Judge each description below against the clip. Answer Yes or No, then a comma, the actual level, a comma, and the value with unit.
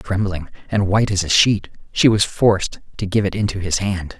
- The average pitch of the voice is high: No, low, 100 Hz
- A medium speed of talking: No, fast, 215 wpm